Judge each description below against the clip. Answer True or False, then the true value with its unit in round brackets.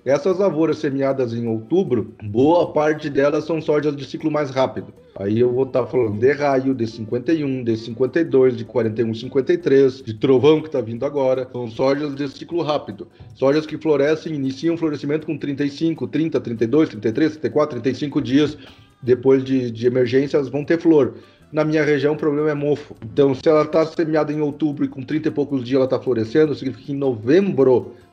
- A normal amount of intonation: True (3.0 semitones)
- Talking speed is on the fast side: True (190 wpm)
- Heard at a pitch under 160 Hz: True (140 Hz)